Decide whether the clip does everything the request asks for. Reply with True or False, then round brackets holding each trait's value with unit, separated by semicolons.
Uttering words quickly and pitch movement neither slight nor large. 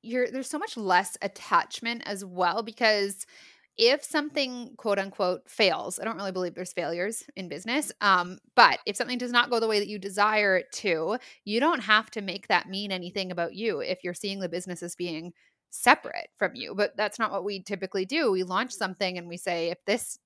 True (210 wpm; 3.8 semitones)